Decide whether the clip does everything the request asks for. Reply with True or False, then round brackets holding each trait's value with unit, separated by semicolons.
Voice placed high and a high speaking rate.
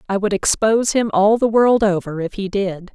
True (205 Hz; 225 wpm)